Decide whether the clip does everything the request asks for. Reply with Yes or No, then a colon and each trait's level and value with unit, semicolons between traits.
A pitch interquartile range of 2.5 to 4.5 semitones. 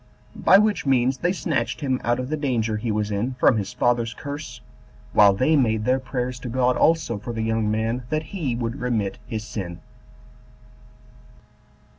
Yes: average, 3.2 semitones